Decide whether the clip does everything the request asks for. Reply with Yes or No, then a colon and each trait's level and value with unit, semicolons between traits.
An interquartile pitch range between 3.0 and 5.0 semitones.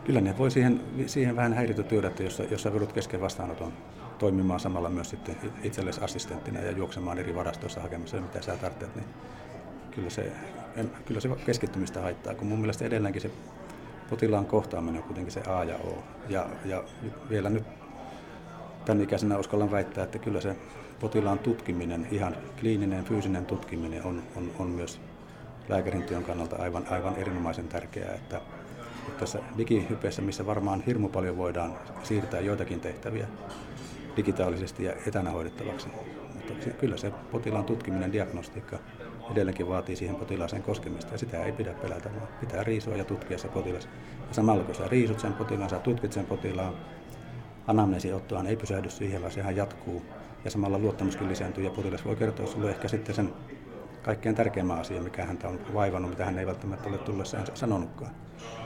Yes: average, 3.3 semitones